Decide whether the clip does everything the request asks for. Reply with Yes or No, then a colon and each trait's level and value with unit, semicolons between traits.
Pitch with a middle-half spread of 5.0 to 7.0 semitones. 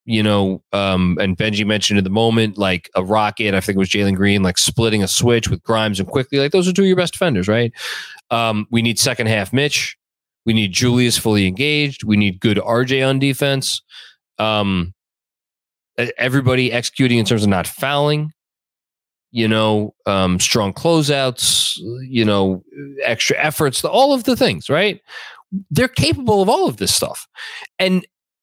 Yes: wide, 5.4 semitones